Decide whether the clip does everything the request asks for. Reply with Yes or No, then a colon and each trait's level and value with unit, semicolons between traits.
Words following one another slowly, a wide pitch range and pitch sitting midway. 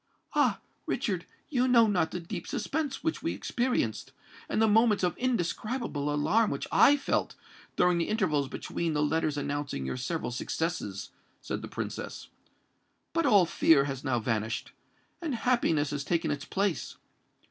No: average, 150 wpm; wide, 7.8 semitones; medium, 170 Hz